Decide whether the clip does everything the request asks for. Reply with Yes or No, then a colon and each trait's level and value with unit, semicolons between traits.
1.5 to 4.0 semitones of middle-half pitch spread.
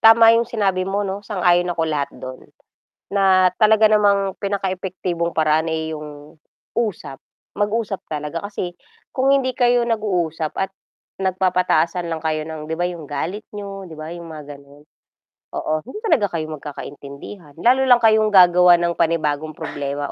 No: average, 4.6 semitones